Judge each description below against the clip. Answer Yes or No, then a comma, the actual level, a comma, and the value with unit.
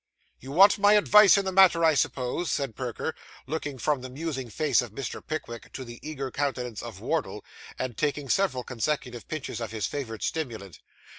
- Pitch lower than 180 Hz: Yes, medium, 140 Hz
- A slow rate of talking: No, average, 180 wpm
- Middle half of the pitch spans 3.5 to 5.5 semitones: Yes, average, 4.5 semitones